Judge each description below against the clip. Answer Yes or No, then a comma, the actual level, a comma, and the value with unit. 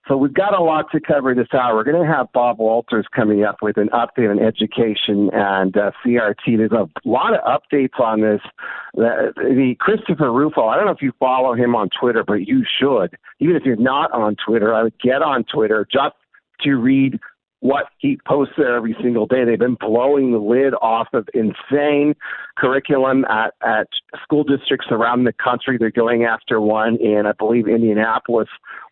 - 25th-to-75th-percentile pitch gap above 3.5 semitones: Yes, average, 4.1 semitones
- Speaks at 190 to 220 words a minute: Yes, average, 195 wpm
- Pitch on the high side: No, low, 120 Hz